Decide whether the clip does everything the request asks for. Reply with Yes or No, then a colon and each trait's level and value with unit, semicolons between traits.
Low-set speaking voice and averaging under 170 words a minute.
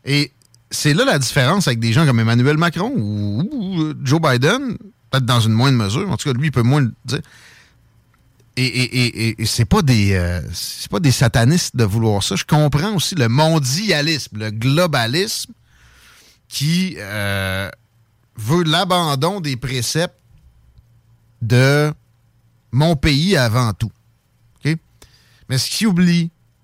Yes: low, 125 Hz; average, 150 wpm